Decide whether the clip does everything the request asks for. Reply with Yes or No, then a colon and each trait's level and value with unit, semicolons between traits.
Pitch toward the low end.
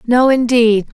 No: high, 235 Hz